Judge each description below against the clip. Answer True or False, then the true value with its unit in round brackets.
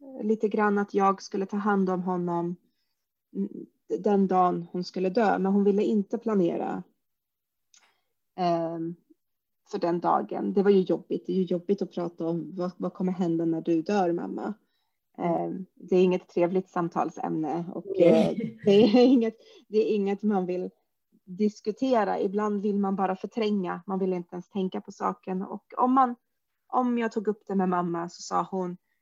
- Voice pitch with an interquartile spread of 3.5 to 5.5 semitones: False (2.9 semitones)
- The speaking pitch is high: True (195 Hz)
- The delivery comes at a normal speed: True (175 wpm)